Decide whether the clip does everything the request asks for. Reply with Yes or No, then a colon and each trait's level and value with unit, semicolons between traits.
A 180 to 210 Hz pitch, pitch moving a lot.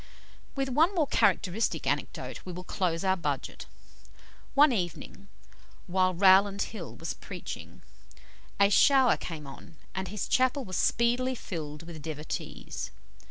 Yes: high, 190 Hz; wide, 6.5 semitones